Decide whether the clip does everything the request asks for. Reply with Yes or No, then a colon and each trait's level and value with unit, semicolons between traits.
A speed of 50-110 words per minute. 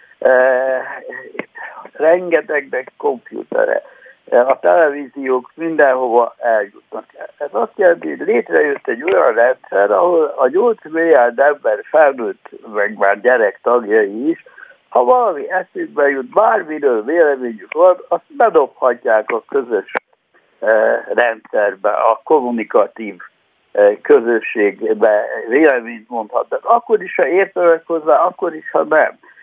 Yes: slow, 105 wpm